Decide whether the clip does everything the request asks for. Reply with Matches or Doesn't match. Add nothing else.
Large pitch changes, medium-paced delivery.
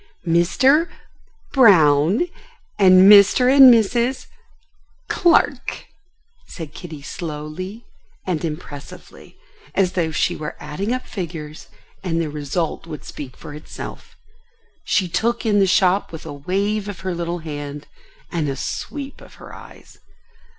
Doesn't match